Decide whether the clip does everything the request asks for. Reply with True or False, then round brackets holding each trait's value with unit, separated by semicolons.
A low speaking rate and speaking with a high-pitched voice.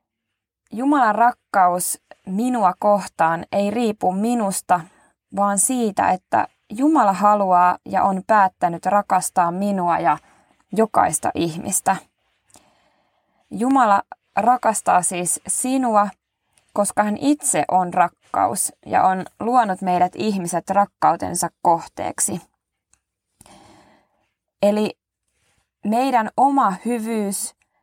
True (85 wpm; 200 Hz)